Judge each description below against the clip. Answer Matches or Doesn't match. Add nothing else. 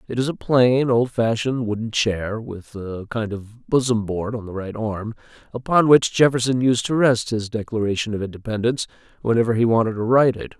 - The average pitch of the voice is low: Matches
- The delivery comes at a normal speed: Matches